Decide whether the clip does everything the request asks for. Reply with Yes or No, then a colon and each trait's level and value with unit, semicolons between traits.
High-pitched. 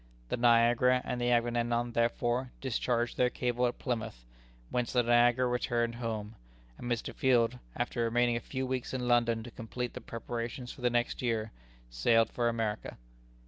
No: low, 120 Hz